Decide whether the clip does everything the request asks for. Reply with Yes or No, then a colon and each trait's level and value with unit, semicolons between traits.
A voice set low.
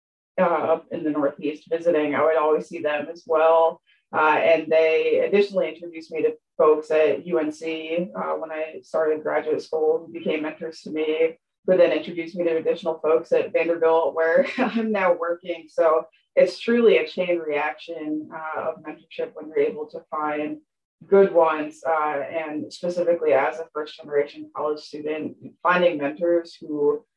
No: medium, 160 Hz